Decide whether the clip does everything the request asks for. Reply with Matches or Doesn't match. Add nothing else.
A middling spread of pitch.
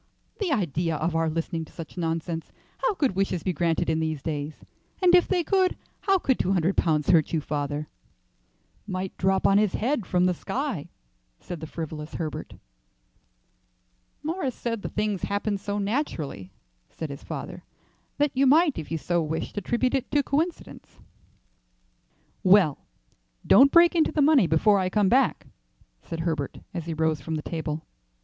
Doesn't match